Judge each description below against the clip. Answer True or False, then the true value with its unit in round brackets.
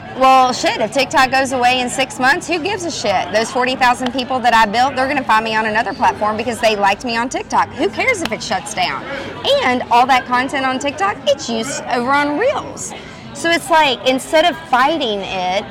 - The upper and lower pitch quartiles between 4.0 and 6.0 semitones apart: False (3.3 semitones)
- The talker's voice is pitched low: False (255 Hz)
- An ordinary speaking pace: False (215 wpm)